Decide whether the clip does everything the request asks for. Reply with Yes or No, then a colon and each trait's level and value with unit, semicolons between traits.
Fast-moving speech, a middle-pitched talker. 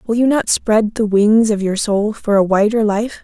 No: fast, 240 wpm; high, 215 Hz